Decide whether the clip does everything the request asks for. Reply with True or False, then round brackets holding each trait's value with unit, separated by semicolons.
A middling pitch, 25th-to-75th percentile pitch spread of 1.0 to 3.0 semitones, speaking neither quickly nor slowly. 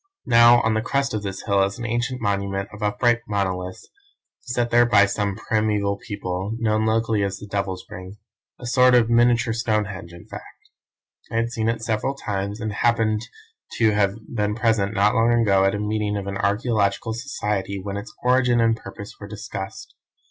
False (105 Hz; 2.7 semitones; 185 wpm)